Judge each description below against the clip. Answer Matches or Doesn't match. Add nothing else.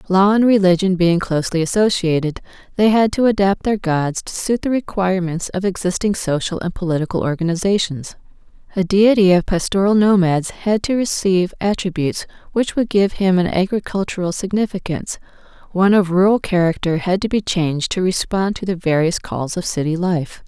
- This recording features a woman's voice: Matches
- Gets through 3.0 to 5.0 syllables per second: Doesn't match